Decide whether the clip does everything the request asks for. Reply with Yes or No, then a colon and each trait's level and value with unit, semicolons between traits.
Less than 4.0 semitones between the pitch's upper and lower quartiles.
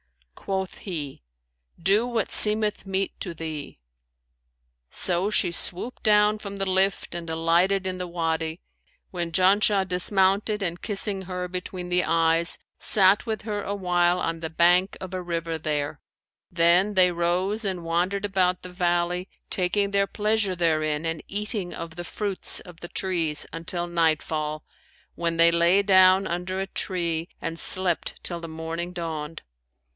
Yes: narrow, 2.6 semitones